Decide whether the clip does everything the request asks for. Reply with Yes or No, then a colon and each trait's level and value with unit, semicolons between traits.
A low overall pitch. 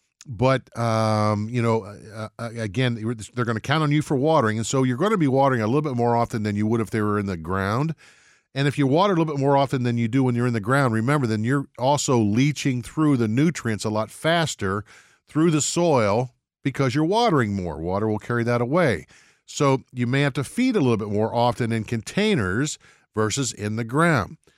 Yes: low, 125 Hz